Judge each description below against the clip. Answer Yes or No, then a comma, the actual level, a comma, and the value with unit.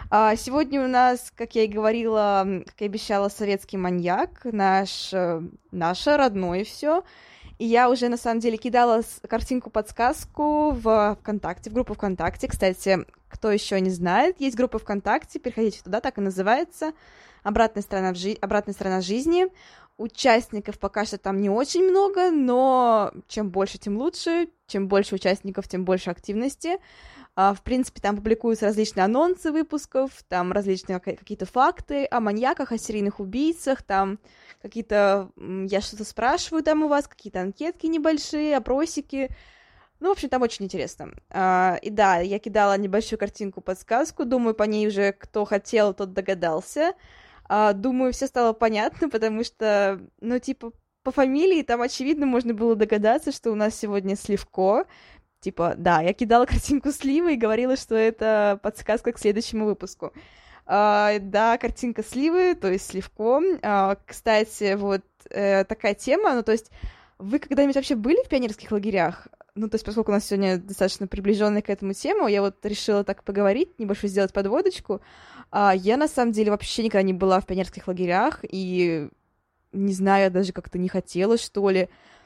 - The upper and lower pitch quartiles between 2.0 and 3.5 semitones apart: No, average, 4.3 semitones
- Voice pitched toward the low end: No, high, 215 Hz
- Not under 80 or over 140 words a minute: No, average, 155 wpm